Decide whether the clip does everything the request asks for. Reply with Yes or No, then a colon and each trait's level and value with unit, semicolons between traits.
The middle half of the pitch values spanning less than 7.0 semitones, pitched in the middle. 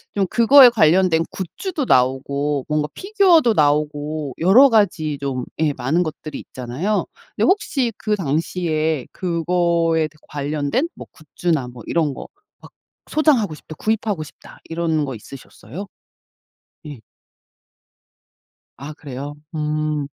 Yes: average, 5.2 semitones; medium, 155 Hz